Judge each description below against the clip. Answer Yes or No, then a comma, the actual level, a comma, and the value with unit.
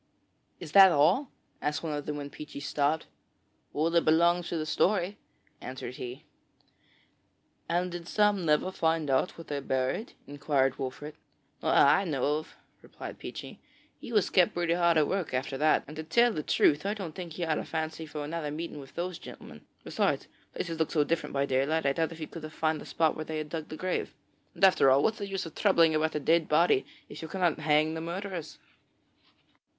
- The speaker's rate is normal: No, fast, 210 wpm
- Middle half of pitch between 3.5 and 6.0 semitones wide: No, average, 2.7 semitones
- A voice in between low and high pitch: Yes, medium, 160 Hz